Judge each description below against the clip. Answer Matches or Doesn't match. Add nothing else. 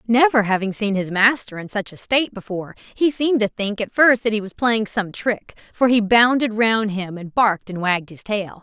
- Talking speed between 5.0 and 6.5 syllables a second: Matches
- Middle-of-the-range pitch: Doesn't match